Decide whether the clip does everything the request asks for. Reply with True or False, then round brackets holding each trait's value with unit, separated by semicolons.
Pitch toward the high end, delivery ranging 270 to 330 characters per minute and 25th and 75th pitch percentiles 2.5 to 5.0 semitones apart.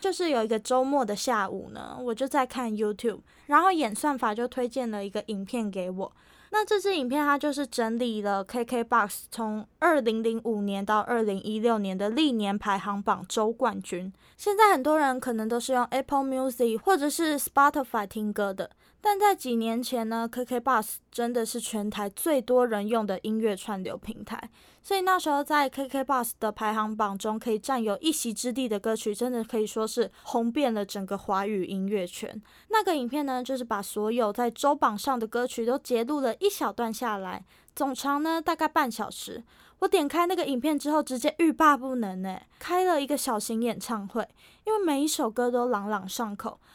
True (240 Hz; 320 characters per minute; 4.7 semitones)